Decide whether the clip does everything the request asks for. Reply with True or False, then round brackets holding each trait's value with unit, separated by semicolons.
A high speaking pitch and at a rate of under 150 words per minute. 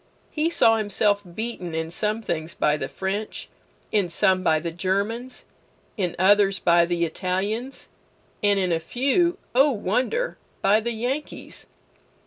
True (200 Hz; 140 wpm)